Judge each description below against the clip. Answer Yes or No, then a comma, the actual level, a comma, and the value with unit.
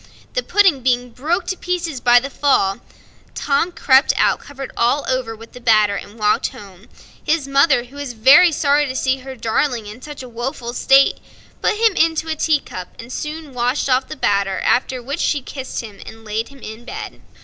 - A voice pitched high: Yes, very high, 260 Hz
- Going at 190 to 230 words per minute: Yes, average, 195 wpm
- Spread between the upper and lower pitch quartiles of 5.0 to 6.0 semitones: No, average, 4.1 semitones